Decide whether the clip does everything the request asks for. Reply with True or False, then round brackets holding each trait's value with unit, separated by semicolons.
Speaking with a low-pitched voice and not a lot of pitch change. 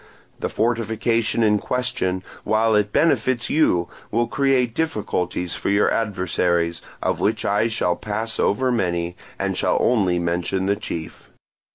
False (105 Hz; 4.4 semitones)